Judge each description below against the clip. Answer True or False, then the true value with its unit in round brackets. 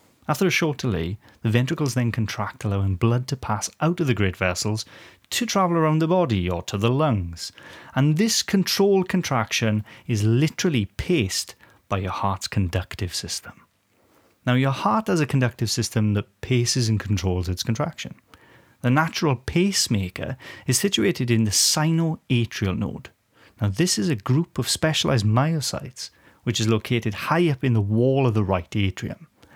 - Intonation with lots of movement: True (6.7 semitones)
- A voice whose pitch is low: True (115 Hz)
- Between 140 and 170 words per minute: True (160 wpm)